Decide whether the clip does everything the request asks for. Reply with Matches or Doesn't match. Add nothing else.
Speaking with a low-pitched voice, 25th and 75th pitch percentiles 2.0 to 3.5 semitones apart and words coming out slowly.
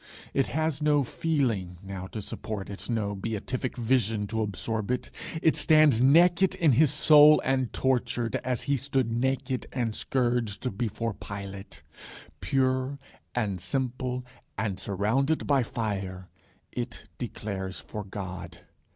Doesn't match